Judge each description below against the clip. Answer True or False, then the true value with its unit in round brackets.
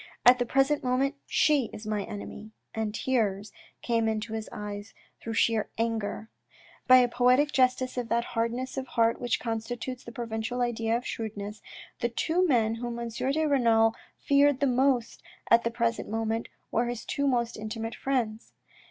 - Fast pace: False (170 wpm)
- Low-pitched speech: False (235 Hz)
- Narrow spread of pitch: True (2.2 semitones)